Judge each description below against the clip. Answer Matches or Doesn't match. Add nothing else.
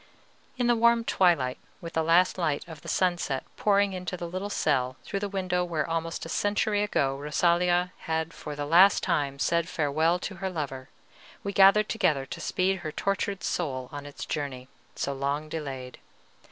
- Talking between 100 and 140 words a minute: Doesn't match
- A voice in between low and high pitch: Matches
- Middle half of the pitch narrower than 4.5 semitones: Doesn't match